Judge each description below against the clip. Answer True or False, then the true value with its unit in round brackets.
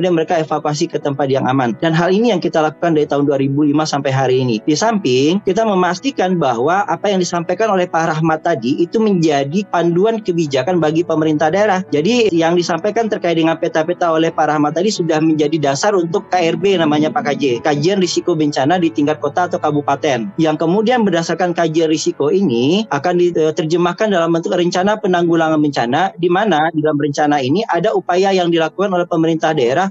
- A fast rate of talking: True (180 wpm)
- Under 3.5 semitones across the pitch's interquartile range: True (2.8 semitones)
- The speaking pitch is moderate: True (170 Hz)